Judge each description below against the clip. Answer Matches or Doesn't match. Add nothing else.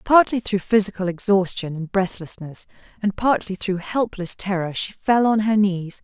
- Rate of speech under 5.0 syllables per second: Matches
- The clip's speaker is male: Doesn't match